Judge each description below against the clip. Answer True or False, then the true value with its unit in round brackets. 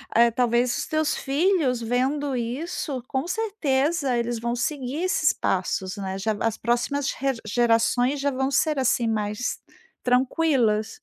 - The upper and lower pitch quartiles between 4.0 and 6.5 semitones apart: False (3.6 semitones)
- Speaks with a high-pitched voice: True (250 Hz)